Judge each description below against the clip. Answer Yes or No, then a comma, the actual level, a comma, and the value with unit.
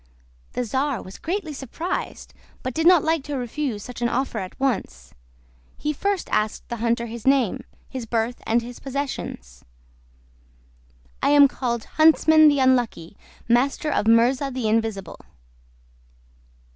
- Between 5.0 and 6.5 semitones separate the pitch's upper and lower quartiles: No, average, 4.1 semitones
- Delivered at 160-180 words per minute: No, average, 140 wpm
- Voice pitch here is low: No, very high, 250 Hz